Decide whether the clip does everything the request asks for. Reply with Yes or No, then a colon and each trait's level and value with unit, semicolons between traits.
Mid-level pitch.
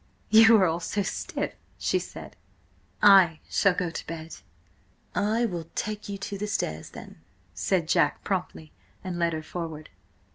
Yes: medium, 180 Hz